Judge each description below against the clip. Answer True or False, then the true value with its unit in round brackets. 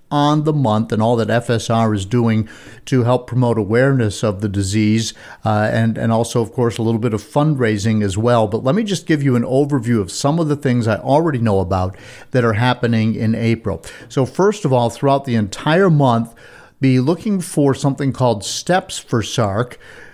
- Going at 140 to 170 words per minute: False (200 wpm)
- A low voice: True (120 Hz)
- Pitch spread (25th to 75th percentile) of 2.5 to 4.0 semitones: True (3.7 semitones)